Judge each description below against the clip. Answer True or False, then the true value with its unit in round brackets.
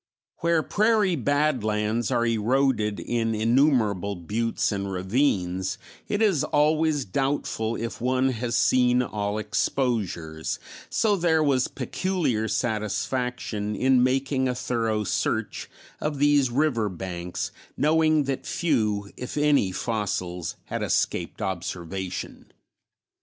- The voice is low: True (120 Hz)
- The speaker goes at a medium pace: False (110 wpm)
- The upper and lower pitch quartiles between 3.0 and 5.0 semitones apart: False (5.6 semitones)